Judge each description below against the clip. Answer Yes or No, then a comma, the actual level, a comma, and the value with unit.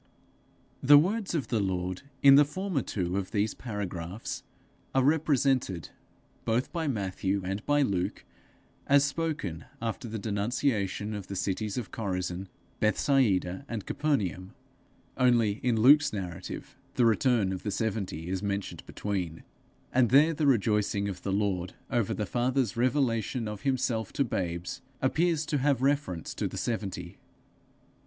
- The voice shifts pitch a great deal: Yes, wide, 5.8 semitones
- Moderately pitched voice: No, low, 110 Hz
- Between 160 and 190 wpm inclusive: No, average, 145 wpm